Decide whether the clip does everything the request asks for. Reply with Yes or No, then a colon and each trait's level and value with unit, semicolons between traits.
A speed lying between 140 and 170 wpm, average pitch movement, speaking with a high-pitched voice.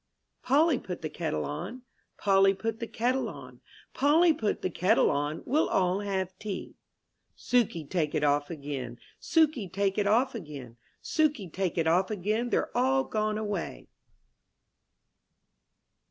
No: average, 150 wpm; wide, 6.7 semitones; high, 195 Hz